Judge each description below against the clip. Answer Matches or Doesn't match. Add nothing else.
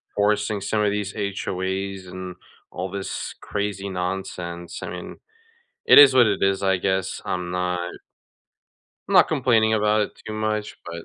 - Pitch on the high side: Doesn't match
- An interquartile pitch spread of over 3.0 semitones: Doesn't match